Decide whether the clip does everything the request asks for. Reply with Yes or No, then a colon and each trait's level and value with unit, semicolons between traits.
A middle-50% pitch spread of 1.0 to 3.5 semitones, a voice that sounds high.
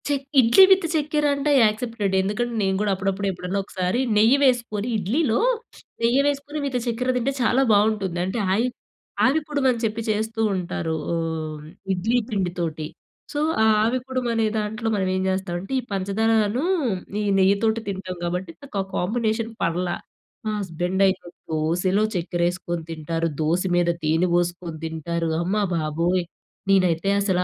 No: average, 4.7 semitones; high, 195 Hz